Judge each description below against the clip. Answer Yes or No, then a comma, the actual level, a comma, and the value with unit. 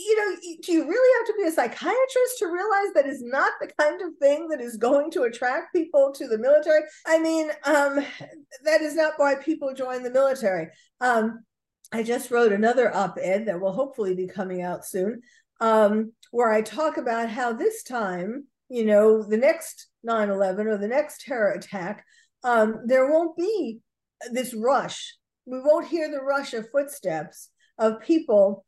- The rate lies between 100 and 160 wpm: No, average, 180 wpm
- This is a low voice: No, very high, 270 Hz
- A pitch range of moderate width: No, wide, 6.0 semitones